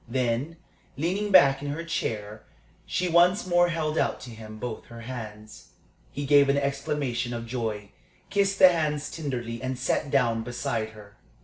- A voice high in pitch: No, low, 130 Hz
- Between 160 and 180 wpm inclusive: Yes, average, 165 wpm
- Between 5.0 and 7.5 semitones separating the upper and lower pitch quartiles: Yes, wide, 5.5 semitones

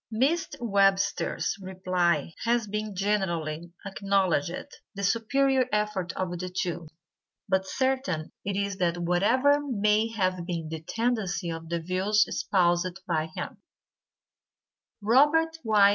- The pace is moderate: No, slow, 120 wpm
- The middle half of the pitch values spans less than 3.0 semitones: No, average, 4.0 semitones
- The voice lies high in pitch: Yes, high, 195 Hz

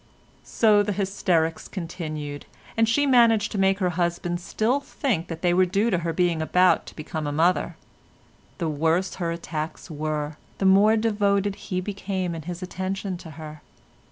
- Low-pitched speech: No, medium, 180 Hz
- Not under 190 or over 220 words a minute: No, average, 170 wpm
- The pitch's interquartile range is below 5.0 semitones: Yes, average, 3.6 semitones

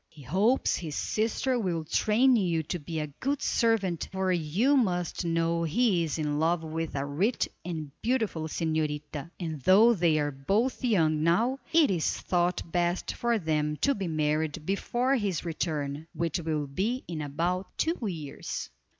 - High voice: No, medium, 170 Hz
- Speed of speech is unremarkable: Yes, average, 165 wpm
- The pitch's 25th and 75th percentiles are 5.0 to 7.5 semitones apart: Yes, average, 5.3 semitones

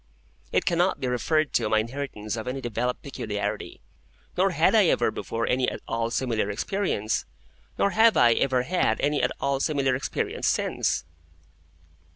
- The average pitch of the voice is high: No, low, 125 Hz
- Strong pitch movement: No, average, 3.9 semitones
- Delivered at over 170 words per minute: No, average, 160 wpm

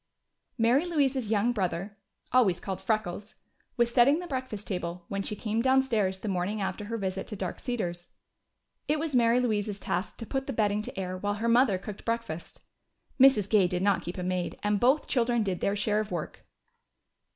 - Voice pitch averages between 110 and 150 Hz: No, high, 210 Hz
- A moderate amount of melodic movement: Yes, average, 4.1 semitones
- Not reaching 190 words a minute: No, average, 195 wpm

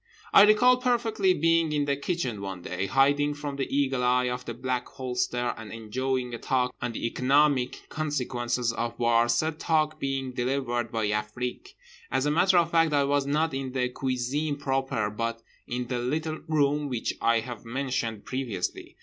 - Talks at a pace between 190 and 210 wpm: No, average, 175 wpm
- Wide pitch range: No, average, 3.5 semitones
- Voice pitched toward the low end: Yes, low, 130 Hz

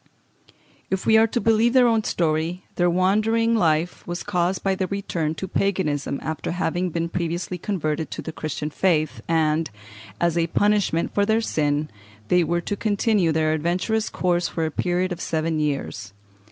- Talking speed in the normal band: Yes, average, 170 wpm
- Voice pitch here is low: No, medium, 175 Hz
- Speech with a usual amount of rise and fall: Yes, average, 3.9 semitones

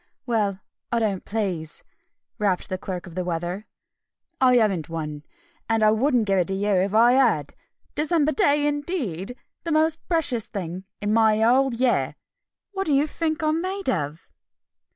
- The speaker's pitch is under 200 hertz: No, high, 220 Hz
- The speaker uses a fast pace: No, average, 165 wpm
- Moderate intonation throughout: No, wide, 7.7 semitones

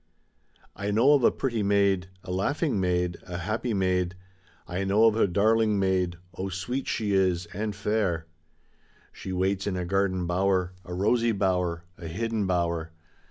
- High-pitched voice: No, very low, 95 Hz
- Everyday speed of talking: Yes, average, 160 wpm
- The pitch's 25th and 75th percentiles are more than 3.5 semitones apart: No, average, 2.7 semitones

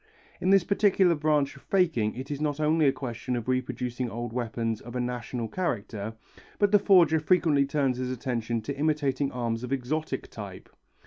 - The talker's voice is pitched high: No, low, 130 Hz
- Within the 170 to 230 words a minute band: Yes, average, 180 wpm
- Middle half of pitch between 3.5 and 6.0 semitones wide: Yes, average, 4.3 semitones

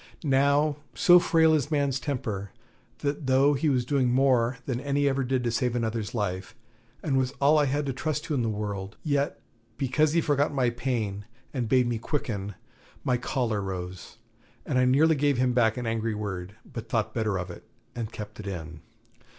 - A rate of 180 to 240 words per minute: Yes, average, 190 wpm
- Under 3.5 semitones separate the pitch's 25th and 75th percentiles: No, average, 4.6 semitones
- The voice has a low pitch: Yes, low, 125 Hz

